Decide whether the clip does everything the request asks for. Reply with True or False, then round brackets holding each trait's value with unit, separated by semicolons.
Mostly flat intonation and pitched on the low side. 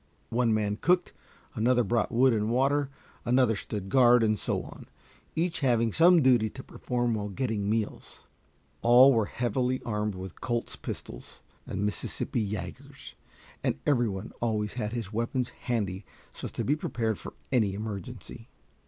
False (3.1 semitones; 115 Hz)